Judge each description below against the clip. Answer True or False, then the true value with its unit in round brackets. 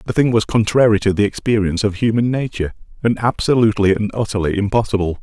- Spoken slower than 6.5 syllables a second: False (6.7 syllables/s)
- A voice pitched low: True (105 Hz)